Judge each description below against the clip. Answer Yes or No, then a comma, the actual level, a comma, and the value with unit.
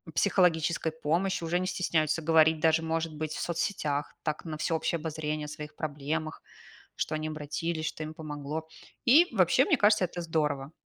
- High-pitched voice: No, medium, 160 Hz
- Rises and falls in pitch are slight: Yes, narrow, 1.6 semitones